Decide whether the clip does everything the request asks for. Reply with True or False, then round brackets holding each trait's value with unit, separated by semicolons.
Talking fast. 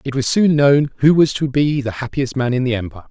True (270 wpm)